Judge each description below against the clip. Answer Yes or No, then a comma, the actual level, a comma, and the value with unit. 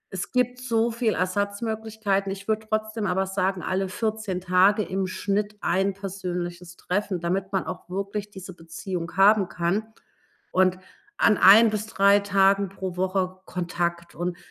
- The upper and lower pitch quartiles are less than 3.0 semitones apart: Yes, narrow, 2.4 semitones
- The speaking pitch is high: Yes, high, 195 Hz